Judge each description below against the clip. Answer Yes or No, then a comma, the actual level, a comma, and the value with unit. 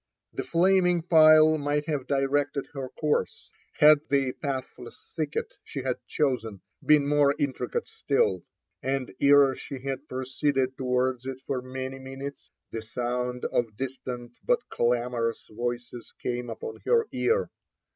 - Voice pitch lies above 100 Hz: Yes, low, 135 Hz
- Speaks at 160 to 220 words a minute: No, slow, 135 wpm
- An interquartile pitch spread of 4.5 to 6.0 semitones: No, average, 2.9 semitones